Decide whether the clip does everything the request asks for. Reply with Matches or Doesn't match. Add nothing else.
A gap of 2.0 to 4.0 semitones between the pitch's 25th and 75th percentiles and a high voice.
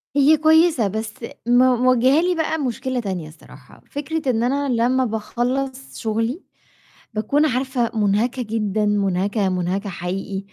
Doesn't match